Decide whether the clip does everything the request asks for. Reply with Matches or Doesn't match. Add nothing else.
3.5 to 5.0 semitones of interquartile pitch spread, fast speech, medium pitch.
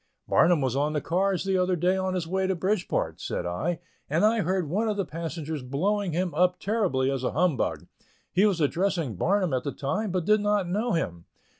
Matches